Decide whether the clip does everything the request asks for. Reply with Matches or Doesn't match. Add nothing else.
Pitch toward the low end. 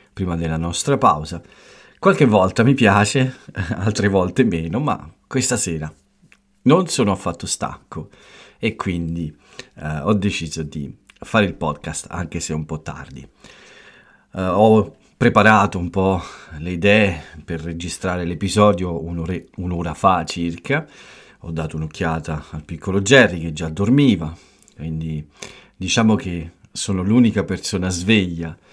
Matches